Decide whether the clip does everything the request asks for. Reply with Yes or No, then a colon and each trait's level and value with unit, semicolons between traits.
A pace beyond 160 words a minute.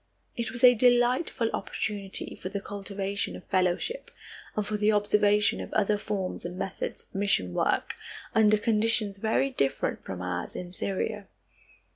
No: average, 150 wpm